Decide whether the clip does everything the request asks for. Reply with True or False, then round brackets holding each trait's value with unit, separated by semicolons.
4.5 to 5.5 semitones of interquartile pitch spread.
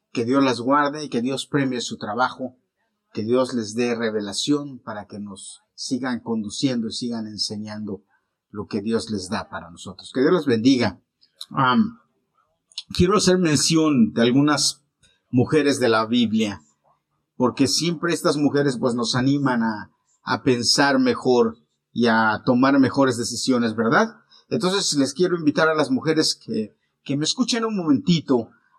True (4.9 semitones)